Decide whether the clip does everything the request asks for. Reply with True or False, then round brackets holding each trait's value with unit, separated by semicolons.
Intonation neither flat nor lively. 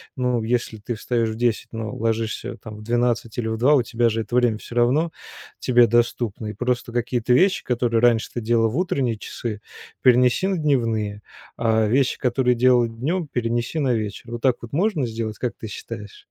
False (1.9 semitones)